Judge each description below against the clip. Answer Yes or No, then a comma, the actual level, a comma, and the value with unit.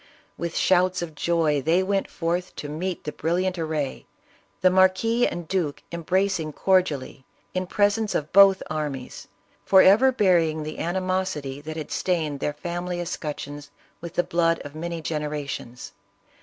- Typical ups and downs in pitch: Yes, average, 3.5 semitones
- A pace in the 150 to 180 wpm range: No, average, 140 wpm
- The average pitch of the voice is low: No, medium, 170 Hz